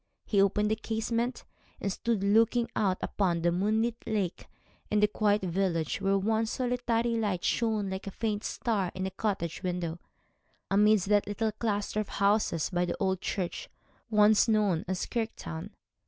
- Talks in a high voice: Yes, high, 205 Hz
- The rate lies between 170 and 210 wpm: No, average, 160 wpm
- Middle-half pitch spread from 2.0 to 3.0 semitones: Yes, average, 2.7 semitones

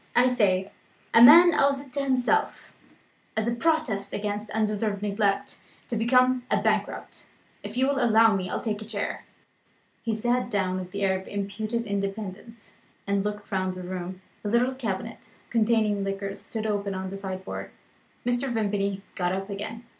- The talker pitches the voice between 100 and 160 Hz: No, high, 210 Hz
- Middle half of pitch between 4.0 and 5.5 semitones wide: No, average, 3.2 semitones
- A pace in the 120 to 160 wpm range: No, average, 170 wpm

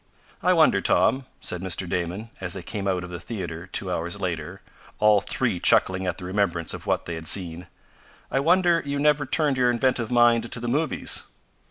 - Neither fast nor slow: Yes, average, 195 wpm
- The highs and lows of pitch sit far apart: Yes, wide, 6.2 semitones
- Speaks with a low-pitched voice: Yes, low, 100 Hz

